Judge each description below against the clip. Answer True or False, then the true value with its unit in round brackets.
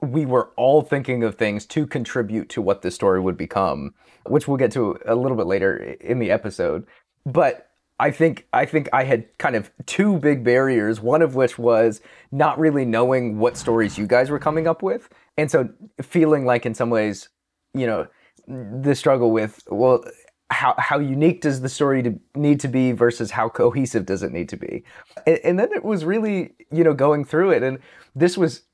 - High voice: False (135 Hz)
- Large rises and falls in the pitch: False (4.7 semitones)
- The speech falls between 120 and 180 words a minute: False (200 wpm)